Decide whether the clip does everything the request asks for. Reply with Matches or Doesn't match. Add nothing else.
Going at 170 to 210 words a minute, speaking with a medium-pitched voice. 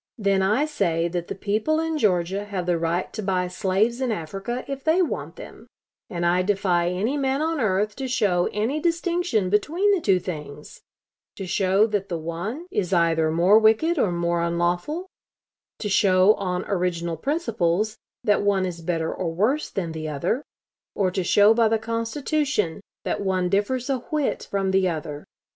Doesn't match